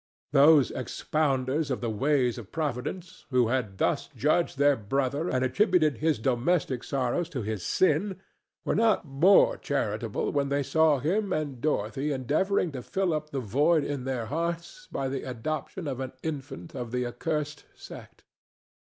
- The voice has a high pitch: No, medium, 140 Hz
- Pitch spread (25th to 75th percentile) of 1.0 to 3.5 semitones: No, average, 4.0 semitones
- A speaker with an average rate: Yes, average, 160 wpm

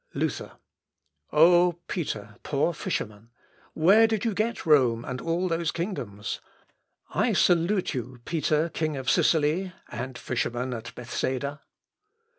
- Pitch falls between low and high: Yes, medium, 155 Hz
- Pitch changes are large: Yes, wide, 5.8 semitones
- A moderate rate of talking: No, slow, 120 wpm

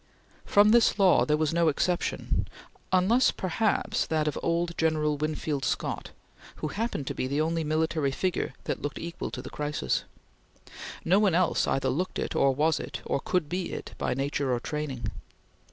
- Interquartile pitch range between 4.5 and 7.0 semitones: No, average, 3.6 semitones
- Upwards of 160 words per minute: Yes, average, 175 wpm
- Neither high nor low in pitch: Yes, medium, 155 Hz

